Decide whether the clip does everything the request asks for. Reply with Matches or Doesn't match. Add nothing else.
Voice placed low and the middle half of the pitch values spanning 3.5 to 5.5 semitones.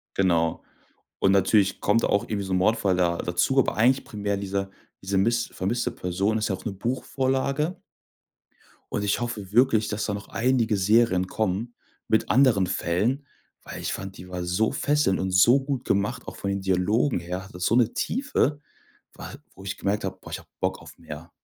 Matches